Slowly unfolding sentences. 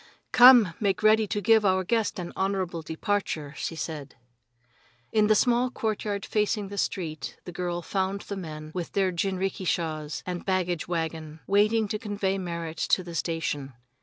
No: average, 160 wpm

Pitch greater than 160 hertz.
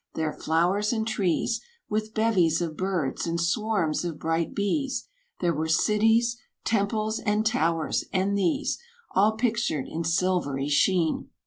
Yes: high, 190 Hz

